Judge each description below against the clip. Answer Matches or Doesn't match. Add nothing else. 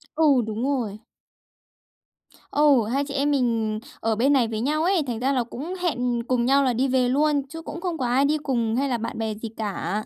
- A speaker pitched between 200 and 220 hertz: Doesn't match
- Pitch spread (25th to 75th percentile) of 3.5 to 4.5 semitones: Matches